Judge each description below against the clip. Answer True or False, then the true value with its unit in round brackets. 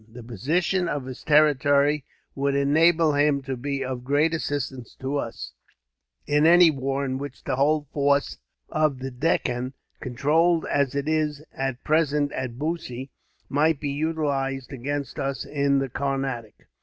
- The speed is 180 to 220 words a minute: False (150 wpm)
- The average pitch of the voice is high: False (140 Hz)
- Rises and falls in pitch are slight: True (2.3 semitones)